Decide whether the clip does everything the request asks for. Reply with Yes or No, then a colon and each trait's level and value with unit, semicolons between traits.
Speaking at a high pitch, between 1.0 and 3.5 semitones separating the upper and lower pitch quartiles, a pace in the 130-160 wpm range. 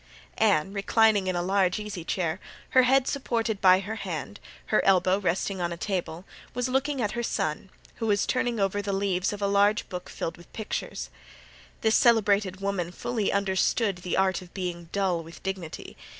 No: high, 195 Hz; average, 2.9 semitones; average, 180 wpm